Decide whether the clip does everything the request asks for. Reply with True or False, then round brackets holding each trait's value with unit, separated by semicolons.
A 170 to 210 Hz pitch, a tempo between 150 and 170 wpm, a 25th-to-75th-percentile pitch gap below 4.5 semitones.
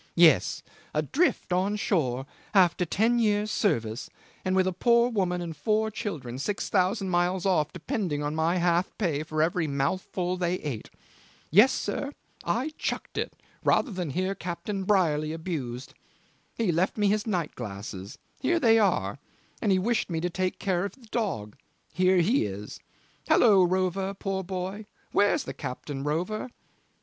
False (185 Hz; 160 wpm; 4.8 semitones)